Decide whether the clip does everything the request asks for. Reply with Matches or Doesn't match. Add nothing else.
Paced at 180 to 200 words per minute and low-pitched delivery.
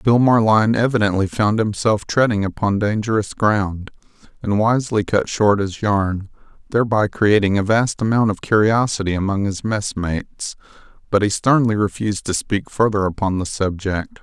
Doesn't match